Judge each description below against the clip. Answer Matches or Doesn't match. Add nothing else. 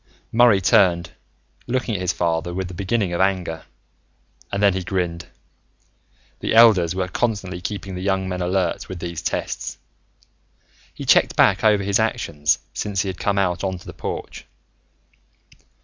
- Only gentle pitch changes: Matches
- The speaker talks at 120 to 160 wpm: Matches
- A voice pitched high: Doesn't match